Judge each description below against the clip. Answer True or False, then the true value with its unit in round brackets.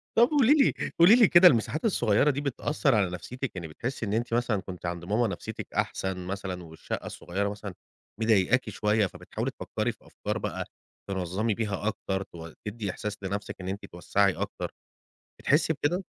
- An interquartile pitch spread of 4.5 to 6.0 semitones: True (5.4 semitones)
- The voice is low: True (105 Hz)